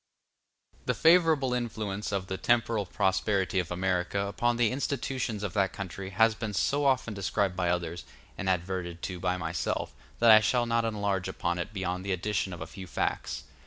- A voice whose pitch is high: No, low, 100 Hz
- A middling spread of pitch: Yes, average, 3.8 semitones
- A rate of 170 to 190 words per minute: Yes, average, 180 wpm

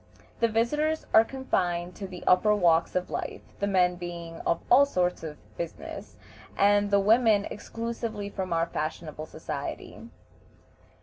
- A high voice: Yes, high, 195 Hz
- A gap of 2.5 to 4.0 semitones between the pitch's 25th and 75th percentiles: No, average, 4.5 semitones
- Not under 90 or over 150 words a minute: Yes, average, 140 wpm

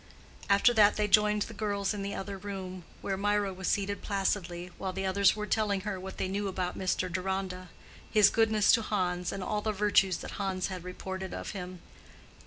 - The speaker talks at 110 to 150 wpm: No, average, 195 wpm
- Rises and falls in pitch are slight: Yes, narrow, 1.8 semitones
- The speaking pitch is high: Yes, high, 195 Hz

